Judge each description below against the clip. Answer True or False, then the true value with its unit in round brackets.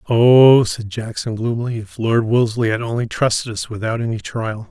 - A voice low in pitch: True (115 Hz)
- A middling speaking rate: True (180 wpm)